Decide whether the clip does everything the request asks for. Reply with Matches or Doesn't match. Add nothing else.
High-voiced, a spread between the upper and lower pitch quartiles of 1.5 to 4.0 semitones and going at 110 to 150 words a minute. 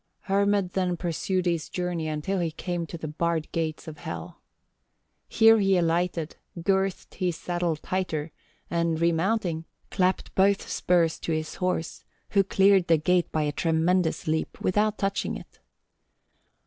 Doesn't match